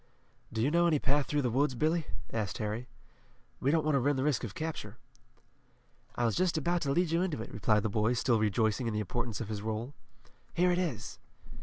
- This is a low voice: Yes, low, 125 Hz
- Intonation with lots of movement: Yes, wide, 5.9 semitones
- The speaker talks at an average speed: No, fast, 220 wpm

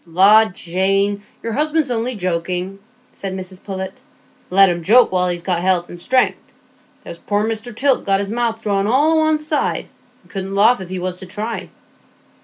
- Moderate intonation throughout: Yes, average, 3.9 semitones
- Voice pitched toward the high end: Yes, high, 195 Hz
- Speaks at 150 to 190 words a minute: Yes, average, 185 wpm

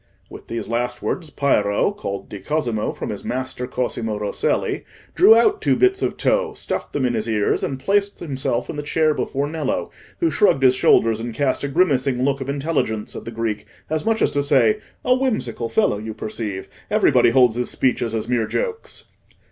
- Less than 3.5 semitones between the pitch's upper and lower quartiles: No, average, 5.3 semitones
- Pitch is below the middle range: Yes, low, 130 Hz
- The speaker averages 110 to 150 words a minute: No, average, 195 wpm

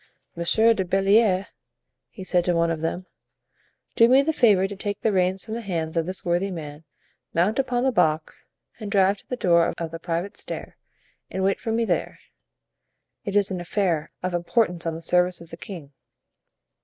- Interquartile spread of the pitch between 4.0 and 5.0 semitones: No, average, 3.4 semitones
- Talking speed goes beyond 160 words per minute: Yes, average, 190 wpm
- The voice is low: No, medium, 185 Hz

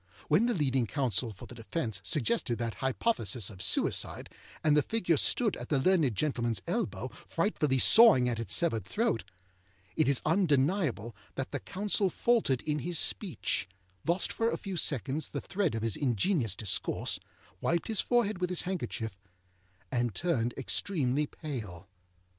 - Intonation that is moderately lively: No, wide, 7.4 semitones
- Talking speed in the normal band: Yes, average, 155 wpm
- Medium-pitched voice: Yes, medium, 145 Hz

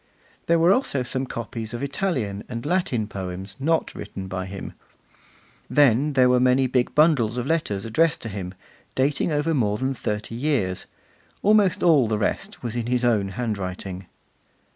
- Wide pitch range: Yes, wide, 5.8 semitones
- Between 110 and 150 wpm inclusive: No, average, 165 wpm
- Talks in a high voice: No, low, 120 Hz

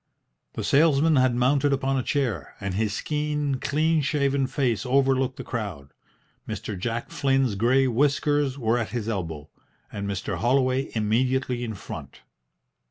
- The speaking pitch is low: Yes, low, 130 Hz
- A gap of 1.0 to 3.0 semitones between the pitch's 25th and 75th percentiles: No, average, 3.9 semitones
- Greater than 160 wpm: No, average, 145 wpm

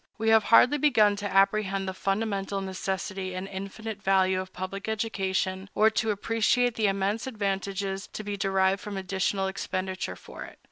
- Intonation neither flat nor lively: No, narrow, 1.9 semitones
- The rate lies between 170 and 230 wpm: No, average, 160 wpm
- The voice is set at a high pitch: Yes, high, 195 Hz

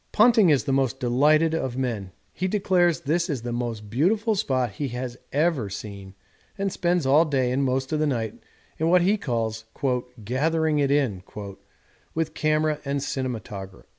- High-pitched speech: No, medium, 140 Hz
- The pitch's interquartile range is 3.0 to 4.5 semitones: No, average, 5.1 semitones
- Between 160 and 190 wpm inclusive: Yes, average, 165 wpm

